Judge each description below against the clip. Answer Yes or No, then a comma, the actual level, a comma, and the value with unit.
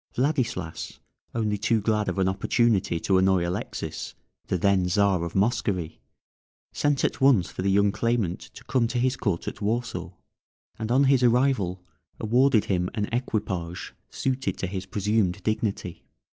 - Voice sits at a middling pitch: No, low, 105 Hz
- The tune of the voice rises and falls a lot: No, average, 4.5 semitones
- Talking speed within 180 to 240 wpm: No, average, 155 wpm